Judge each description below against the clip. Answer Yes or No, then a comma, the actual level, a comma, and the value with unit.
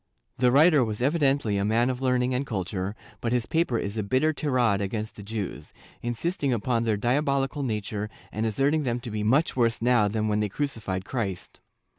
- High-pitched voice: No, low, 120 Hz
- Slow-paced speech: No, average, 190 wpm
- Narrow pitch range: No, average, 4.2 semitones